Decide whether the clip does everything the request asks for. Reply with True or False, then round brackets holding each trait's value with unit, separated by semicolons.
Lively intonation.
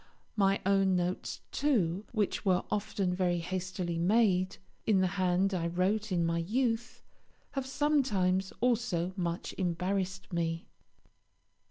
False (2.9 semitones)